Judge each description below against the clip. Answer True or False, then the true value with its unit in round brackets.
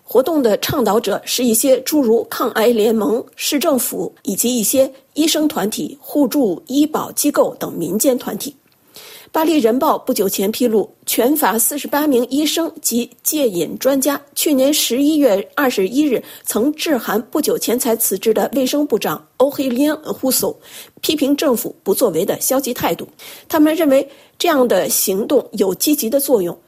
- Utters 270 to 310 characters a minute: False (255 characters per minute)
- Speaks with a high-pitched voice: True (270 Hz)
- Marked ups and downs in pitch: False (3.9 semitones)